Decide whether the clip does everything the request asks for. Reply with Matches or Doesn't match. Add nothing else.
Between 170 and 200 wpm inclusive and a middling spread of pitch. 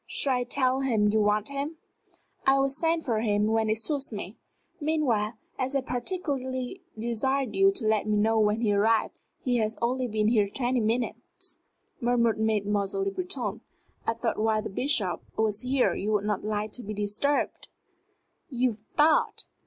Matches